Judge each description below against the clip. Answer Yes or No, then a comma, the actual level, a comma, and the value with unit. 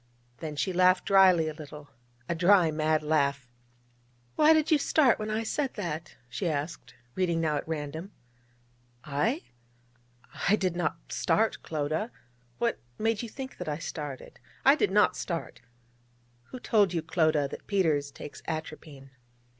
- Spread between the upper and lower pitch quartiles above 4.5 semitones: Yes, average, 5.3 semitones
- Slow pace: No, average, 150 wpm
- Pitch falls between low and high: Yes, medium, 165 Hz